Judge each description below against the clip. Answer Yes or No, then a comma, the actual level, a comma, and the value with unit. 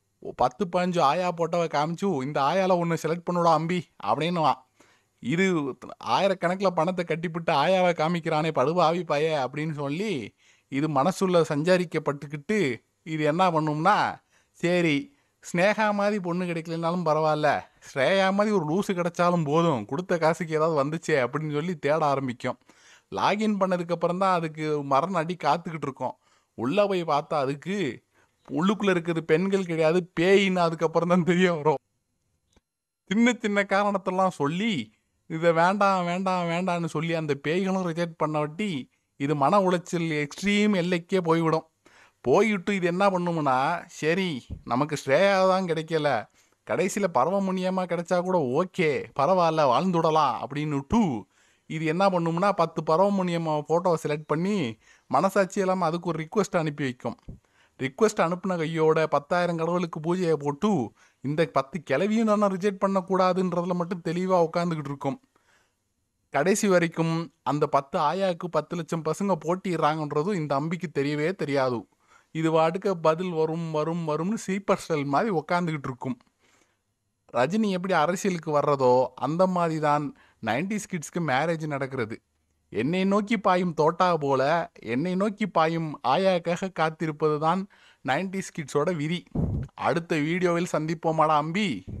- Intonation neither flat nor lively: Yes, average, 3.6 semitones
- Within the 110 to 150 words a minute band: Yes, average, 125 wpm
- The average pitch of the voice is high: No, medium, 170 Hz